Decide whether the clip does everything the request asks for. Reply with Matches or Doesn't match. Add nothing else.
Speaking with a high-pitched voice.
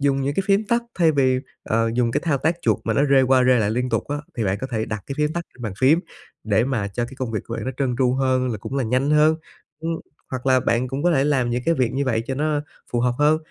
Doesn't match